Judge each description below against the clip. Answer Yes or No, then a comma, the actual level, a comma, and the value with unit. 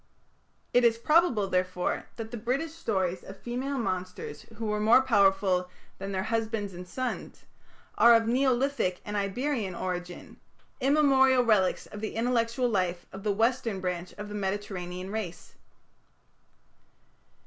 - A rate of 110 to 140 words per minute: Yes, slow, 135 wpm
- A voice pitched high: Yes, high, 210 Hz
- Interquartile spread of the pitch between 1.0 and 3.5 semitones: No, average, 4.5 semitones